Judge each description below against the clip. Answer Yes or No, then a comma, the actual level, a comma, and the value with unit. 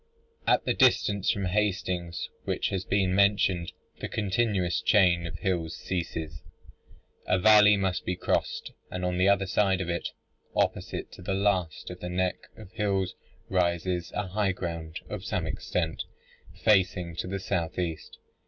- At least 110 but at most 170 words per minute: Yes, average, 155 wpm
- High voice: No, very low, 90 Hz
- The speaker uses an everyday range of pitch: No, narrow, 2.2 semitones